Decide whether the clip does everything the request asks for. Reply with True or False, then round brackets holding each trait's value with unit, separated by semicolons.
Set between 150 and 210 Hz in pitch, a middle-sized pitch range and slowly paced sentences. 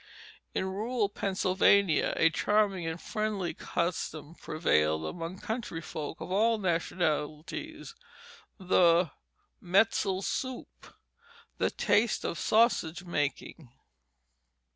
True (185 Hz; 4.3 semitones; 95 wpm)